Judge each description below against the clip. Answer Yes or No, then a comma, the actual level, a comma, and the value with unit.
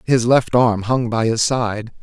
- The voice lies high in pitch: No, low, 115 Hz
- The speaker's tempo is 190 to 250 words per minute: Yes, fast, 205 wpm